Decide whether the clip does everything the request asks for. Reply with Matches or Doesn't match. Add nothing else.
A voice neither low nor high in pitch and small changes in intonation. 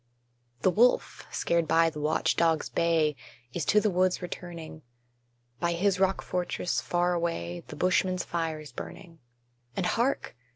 Matches